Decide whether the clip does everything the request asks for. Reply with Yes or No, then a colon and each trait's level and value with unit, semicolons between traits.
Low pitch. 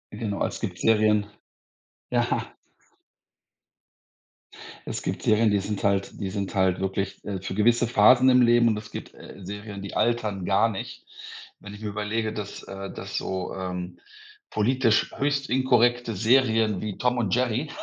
Yes: low, 105 Hz